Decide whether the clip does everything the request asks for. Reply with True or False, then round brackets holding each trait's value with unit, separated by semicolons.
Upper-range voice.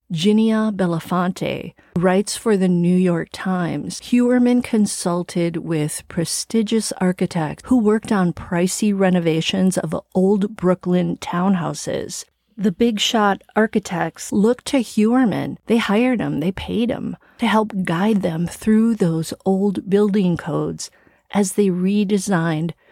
True (195 Hz)